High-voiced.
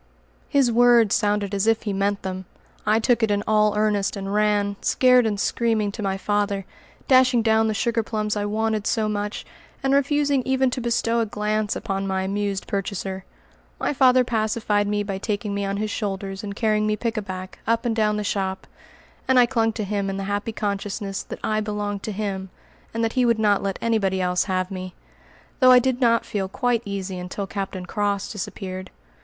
Yes: high, 210 Hz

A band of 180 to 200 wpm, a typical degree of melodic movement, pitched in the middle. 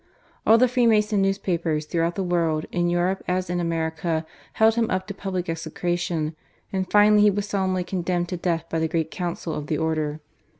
Yes: average, 185 wpm; average, 3.0 semitones; medium, 175 Hz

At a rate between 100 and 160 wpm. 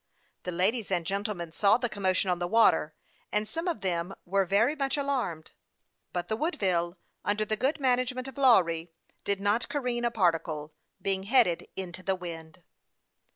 No: average, 170 wpm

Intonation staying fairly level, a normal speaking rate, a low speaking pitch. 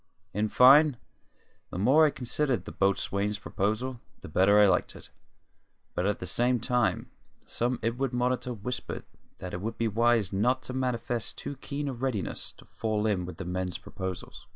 No: average, 4.2 semitones; average, 175 wpm; low, 115 Hz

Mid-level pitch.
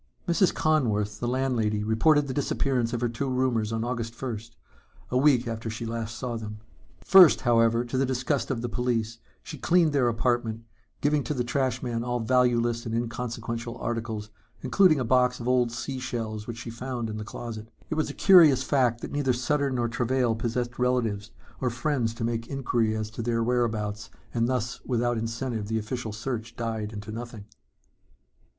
No: low, 120 Hz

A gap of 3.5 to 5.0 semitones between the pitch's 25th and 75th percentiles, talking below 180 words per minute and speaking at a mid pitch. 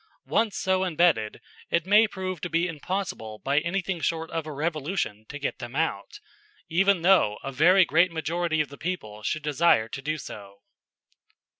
Yes: average, 4.7 semitones; average, 170 wpm; medium, 160 Hz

